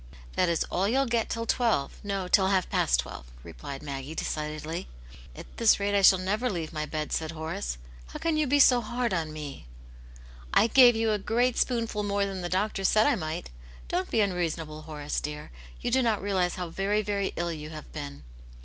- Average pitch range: No, wide, 5.8 semitones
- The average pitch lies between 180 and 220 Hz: Yes, medium, 185 Hz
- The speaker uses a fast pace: Yes, fast, 210 wpm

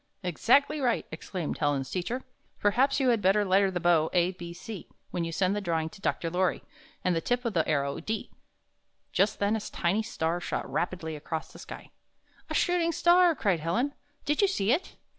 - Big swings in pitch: Yes, wide, 6.1 semitones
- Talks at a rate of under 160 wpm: No, average, 195 wpm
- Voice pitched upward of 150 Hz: Yes, high, 190 Hz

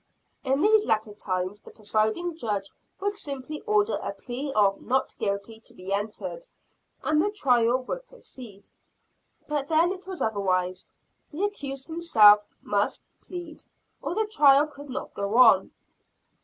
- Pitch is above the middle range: Yes, very high, 265 Hz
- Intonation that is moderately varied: No, wide, 8.4 semitones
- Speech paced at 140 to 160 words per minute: Yes, average, 145 wpm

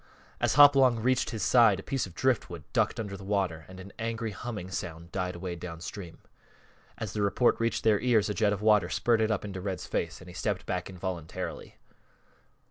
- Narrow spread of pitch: No, average, 3.9 semitones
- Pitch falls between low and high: No, low, 100 Hz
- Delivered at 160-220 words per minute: Yes, average, 195 wpm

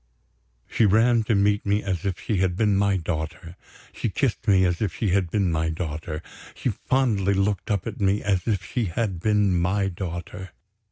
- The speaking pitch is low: Yes, very low, 95 Hz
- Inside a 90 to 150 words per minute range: No, average, 190 wpm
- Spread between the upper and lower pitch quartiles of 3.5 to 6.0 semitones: No, average, 2.8 semitones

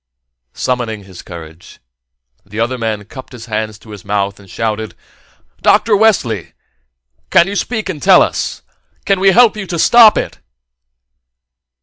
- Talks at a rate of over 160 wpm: No, average, 140 wpm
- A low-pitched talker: Yes, low, 115 Hz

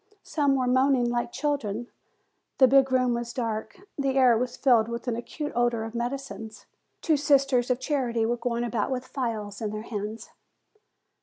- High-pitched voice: Yes, high, 245 Hz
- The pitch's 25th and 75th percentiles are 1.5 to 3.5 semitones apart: Yes, narrow, 2.5 semitones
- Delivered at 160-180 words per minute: Yes, average, 170 wpm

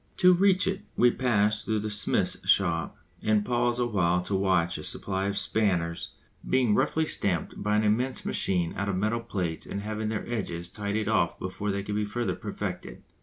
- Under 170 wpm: No, average, 185 wpm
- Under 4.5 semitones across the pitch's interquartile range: Yes, average, 3.5 semitones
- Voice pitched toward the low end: Yes, low, 105 Hz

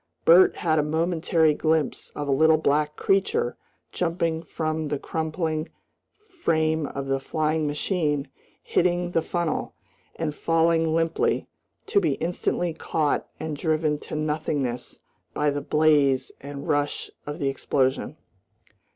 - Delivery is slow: Yes, slow, 130 wpm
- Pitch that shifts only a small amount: Yes, narrow, 2.0 semitones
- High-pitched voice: No, medium, 155 Hz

